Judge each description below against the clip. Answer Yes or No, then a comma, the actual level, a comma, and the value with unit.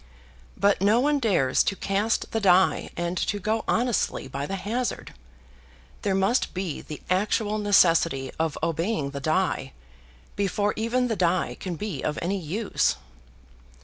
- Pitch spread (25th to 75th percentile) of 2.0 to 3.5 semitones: No, average, 4.3 semitones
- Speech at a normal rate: Yes, average, 145 wpm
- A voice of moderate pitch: No, high, 195 Hz